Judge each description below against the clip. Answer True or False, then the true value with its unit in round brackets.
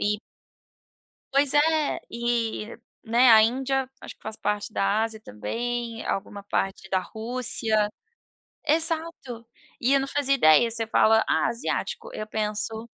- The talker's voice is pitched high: True (230 Hz)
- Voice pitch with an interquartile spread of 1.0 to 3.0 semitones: False (3.7 semitones)